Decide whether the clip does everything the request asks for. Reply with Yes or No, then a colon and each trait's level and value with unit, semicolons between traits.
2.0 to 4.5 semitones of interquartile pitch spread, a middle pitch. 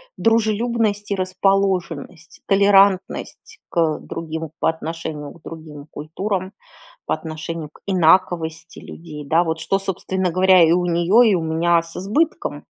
Yes: average, 3.3 semitones; medium, 175 Hz